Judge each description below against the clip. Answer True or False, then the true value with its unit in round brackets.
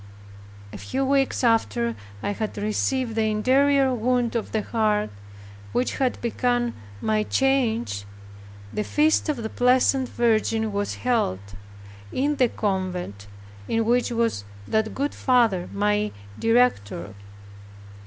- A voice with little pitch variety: False (3.3 semitones)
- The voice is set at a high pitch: True (230 Hz)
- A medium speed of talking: False (125 wpm)